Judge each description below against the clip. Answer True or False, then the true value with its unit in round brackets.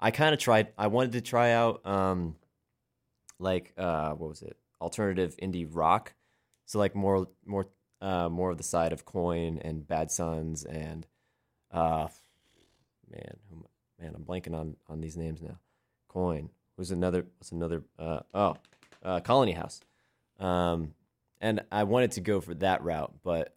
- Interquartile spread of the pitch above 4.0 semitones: False (3.7 semitones)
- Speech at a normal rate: True (160 wpm)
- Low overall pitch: True (90 Hz)